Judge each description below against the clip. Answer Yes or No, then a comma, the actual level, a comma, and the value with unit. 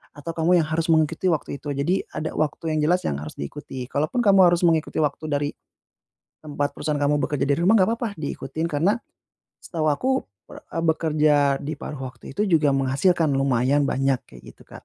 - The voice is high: No, medium, 150 Hz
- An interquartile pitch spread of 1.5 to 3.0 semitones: Yes, average, 2.7 semitones